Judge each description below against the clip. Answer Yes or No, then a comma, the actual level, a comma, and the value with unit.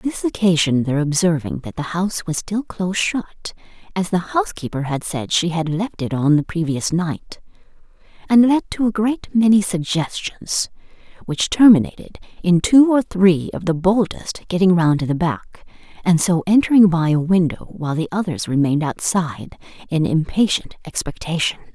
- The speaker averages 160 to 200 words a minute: Yes, average, 165 wpm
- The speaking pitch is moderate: Yes, medium, 180 Hz